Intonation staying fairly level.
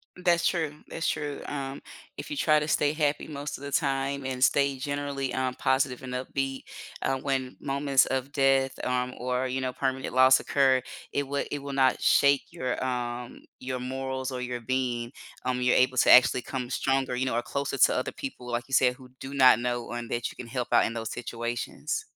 Yes: narrow, 1.8 semitones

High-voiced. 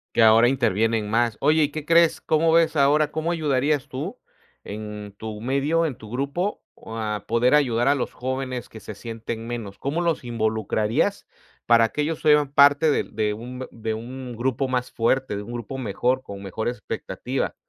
No: low, 125 Hz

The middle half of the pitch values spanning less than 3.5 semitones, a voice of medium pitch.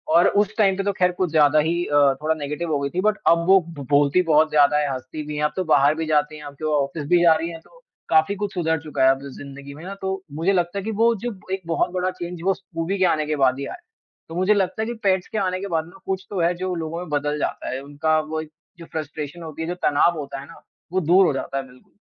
No: average, 3.8 semitones; medium, 160 Hz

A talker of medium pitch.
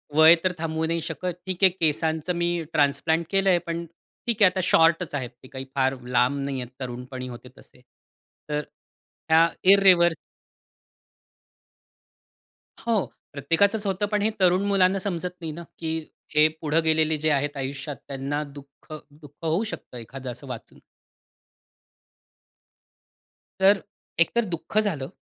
Yes: medium, 160 Hz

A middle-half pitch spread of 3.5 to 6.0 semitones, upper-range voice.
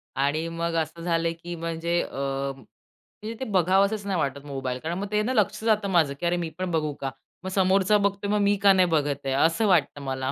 No: average, 5.2 semitones; medium, 170 Hz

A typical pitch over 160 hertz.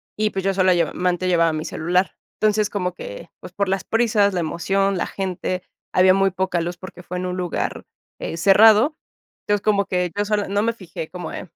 Yes: high, 190 Hz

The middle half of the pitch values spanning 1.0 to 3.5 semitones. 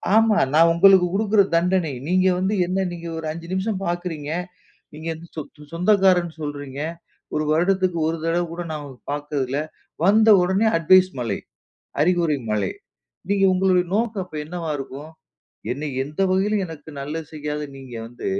No: average, 4.0 semitones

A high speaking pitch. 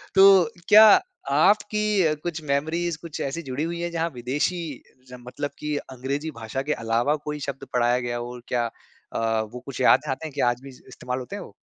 No: medium, 140 Hz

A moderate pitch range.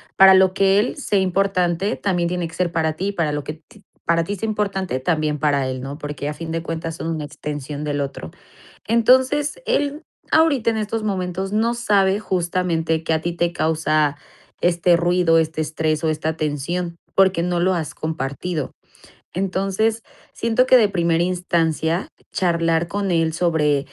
Yes: average, 3.6 semitones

